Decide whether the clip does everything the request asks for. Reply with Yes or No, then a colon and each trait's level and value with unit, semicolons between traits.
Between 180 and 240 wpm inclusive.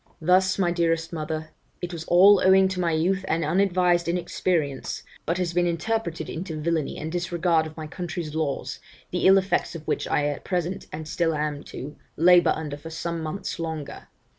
Yes: average, 185 wpm